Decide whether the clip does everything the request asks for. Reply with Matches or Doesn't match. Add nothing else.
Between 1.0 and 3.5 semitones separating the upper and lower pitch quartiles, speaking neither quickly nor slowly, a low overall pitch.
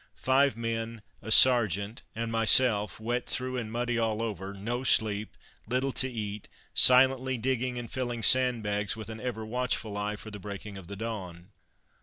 Matches